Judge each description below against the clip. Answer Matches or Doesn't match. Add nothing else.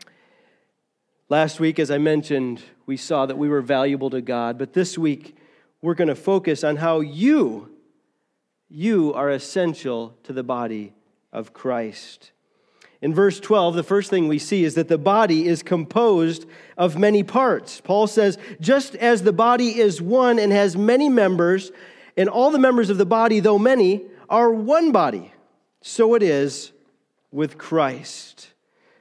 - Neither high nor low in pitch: Matches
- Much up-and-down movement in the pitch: Matches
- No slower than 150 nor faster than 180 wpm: Matches